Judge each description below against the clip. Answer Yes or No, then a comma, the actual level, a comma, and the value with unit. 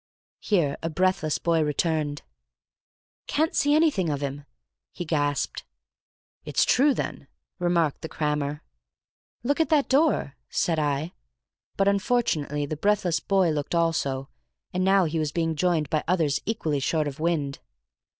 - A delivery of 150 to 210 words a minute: No, average, 140 wpm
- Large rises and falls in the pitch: No, average, 4.3 semitones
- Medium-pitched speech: Yes, medium, 165 Hz